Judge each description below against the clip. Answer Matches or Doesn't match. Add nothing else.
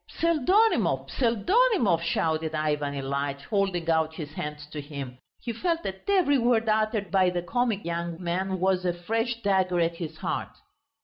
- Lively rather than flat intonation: Matches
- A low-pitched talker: Doesn't match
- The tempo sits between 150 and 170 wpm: Matches